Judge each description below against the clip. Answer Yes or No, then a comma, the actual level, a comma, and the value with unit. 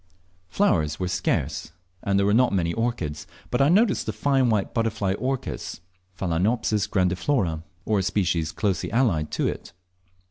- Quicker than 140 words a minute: Yes, average, 150 wpm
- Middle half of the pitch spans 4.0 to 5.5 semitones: Yes, average, 5.0 semitones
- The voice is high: No, low, 100 Hz